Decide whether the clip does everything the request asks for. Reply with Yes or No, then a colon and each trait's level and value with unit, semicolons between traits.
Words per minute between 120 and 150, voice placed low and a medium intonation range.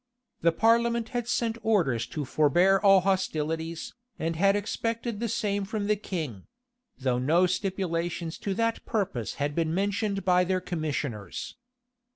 No: average, 145 wpm; medium, 185 Hz; average, 4.6 semitones